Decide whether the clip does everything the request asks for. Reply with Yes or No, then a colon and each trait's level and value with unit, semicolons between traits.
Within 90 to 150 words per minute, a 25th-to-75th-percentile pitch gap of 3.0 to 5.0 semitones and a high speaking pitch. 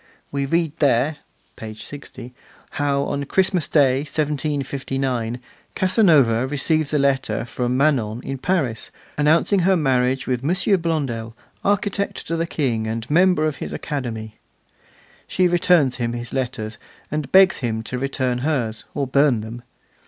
No: average, 140 wpm; average, 4.3 semitones; medium, 140 Hz